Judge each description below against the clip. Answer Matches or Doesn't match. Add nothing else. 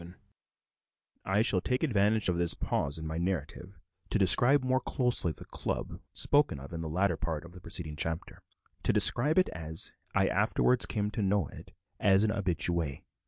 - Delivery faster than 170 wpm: Matches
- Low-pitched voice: Matches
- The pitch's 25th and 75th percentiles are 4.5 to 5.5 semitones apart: Matches